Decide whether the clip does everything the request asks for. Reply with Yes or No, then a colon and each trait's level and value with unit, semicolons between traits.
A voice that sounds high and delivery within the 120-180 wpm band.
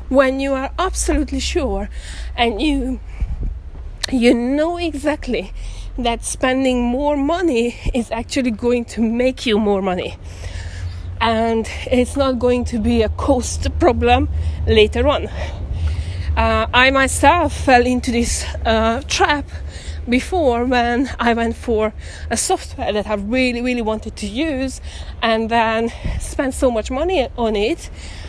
Yes: high, 235 Hz; slow, 135 wpm